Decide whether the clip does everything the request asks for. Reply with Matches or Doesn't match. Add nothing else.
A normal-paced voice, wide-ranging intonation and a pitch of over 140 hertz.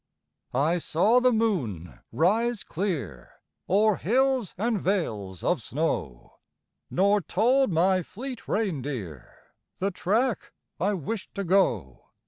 Doesn't match